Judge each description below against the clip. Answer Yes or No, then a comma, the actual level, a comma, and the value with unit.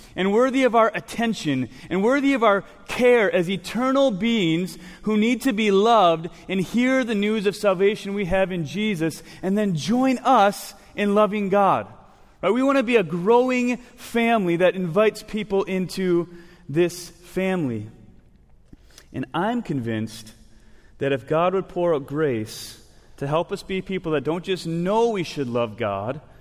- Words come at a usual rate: Yes, average, 165 wpm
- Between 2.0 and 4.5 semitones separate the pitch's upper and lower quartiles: No, average, 5.1 semitones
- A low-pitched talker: No, medium, 185 Hz